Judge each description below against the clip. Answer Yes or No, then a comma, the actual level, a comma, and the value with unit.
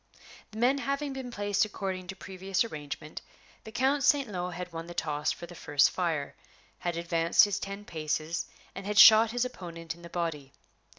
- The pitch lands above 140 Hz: Yes, medium, 185 Hz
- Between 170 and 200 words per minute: Yes, average, 185 wpm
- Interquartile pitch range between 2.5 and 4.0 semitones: No, average, 4.6 semitones